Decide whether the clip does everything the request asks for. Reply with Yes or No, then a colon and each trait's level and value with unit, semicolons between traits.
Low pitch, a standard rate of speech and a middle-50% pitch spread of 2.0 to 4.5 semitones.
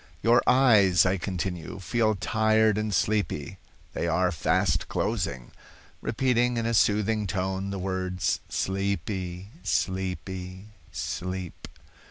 No: very low, 95 Hz; slow, 110 wpm; average, 2.9 semitones